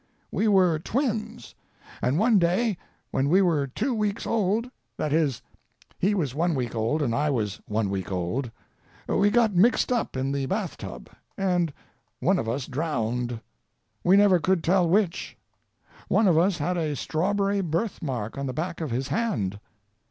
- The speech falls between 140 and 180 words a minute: Yes, average, 160 wpm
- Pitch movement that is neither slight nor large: No, wide, 7.1 semitones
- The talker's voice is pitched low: No, medium, 170 Hz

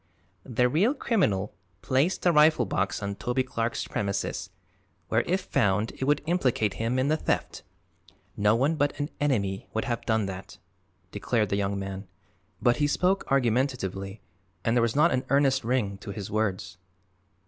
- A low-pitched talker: Yes, low, 120 Hz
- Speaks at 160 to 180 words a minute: Yes, average, 165 wpm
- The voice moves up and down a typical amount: No, wide, 5.9 semitones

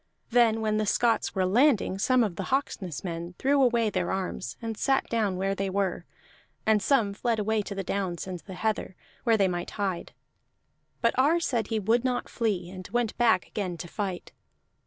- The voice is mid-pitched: No, high, 210 Hz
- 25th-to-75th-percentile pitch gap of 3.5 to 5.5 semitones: Yes, average, 3.8 semitones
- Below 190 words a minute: No, average, 195 wpm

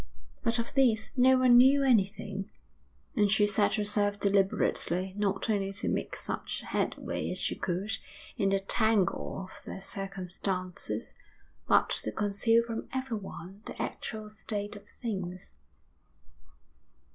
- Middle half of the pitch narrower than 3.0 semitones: Yes, narrow, 2.6 semitones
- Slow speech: Yes, slow, 130 wpm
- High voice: Yes, high, 205 Hz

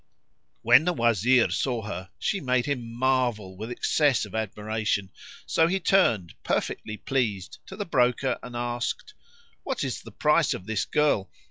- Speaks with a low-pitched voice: Yes, low, 120 Hz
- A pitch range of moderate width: Yes, average, 4.3 semitones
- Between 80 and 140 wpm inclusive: No, average, 155 wpm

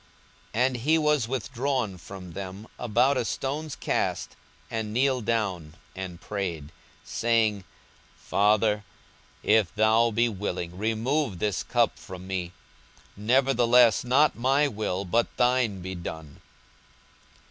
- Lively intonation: No, average, 4.7 semitones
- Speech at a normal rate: No, slow, 125 wpm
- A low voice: Yes, low, 110 Hz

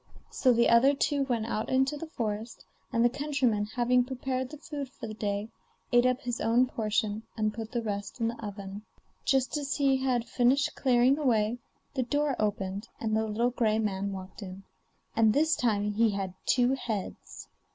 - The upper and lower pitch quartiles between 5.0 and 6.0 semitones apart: No, average, 3.5 semitones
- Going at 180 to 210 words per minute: Yes, average, 185 wpm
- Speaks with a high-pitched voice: Yes, high, 235 Hz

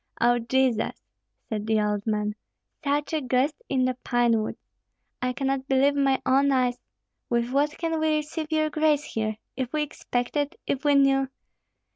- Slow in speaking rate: No, average, 165 wpm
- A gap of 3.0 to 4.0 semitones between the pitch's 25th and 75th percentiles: Yes, average, 3.3 semitones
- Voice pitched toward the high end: Yes, very high, 265 Hz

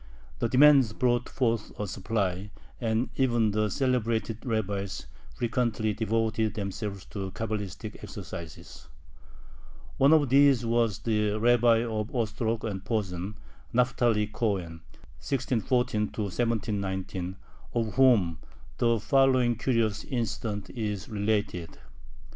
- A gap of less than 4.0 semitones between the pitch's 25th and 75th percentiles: Yes, average, 2.8 semitones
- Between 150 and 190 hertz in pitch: No, low, 110 Hz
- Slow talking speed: Yes, slow, 105 wpm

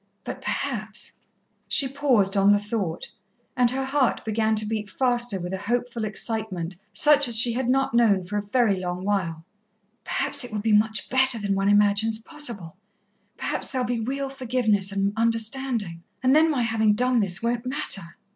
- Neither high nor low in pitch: No, high, 225 Hz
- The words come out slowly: No, average, 180 wpm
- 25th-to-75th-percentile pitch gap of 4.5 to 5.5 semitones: No, average, 3.7 semitones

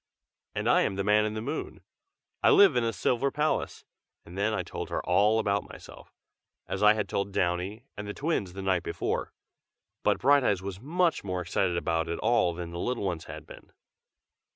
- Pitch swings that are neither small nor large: Yes, average, 4.5 semitones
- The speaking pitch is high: No, low, 100 Hz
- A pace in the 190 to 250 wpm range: Yes, average, 200 wpm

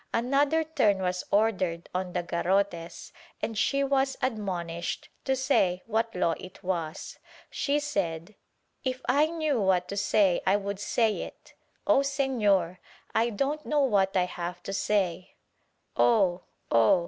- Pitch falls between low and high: No, high, 200 Hz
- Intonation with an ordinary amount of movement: No, wide, 6.5 semitones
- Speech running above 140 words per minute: Yes, average, 150 wpm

